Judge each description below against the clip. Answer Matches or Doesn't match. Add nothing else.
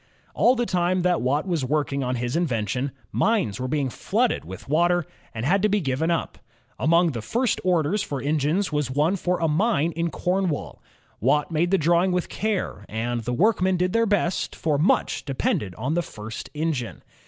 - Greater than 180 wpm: Matches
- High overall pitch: Doesn't match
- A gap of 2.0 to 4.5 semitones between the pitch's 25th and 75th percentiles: Doesn't match